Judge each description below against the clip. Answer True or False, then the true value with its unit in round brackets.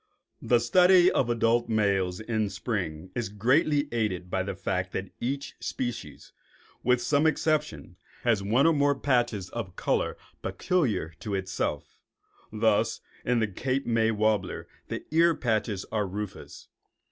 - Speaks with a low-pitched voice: True (115 Hz)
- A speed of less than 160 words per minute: True (140 wpm)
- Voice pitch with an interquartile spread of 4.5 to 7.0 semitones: True (5.0 semitones)